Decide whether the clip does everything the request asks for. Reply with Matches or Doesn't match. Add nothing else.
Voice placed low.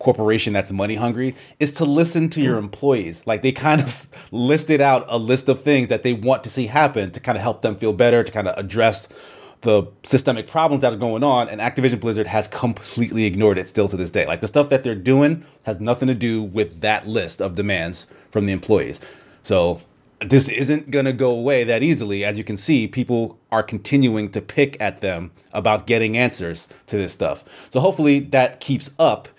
Matches